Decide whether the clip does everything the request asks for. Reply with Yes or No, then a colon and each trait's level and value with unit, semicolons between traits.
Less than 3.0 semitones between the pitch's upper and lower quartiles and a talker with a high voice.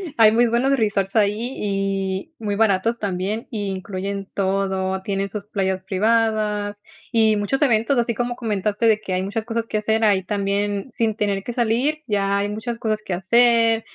Yes: narrow, 2.5 semitones; high, 210 Hz